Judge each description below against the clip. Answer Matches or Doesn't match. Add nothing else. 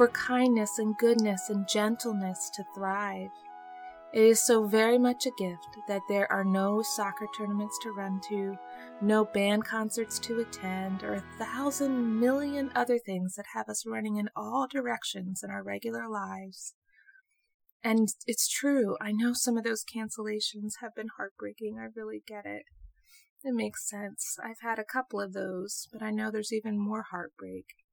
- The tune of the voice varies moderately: Matches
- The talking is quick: Doesn't match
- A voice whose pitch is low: Doesn't match